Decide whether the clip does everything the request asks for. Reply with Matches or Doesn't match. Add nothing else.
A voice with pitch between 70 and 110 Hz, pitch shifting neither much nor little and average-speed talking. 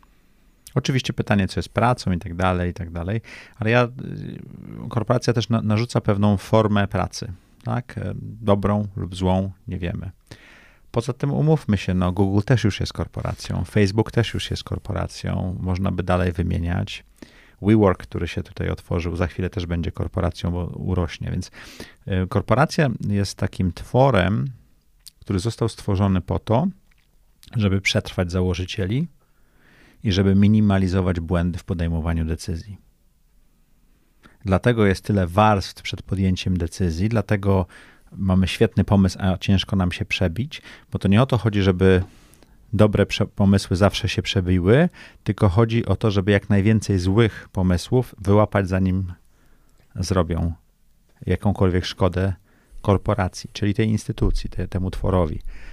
Matches